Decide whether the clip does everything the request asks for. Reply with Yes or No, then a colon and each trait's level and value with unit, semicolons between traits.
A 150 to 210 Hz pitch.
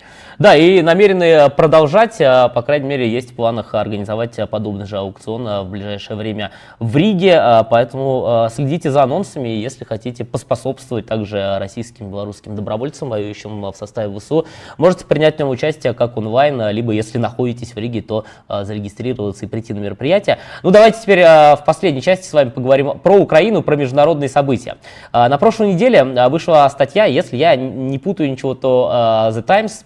No: low, 125 Hz